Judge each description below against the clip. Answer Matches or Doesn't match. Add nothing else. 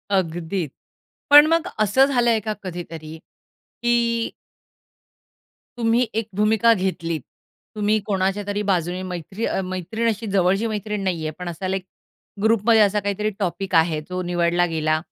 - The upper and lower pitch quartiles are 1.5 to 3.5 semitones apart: Doesn't match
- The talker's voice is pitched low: Doesn't match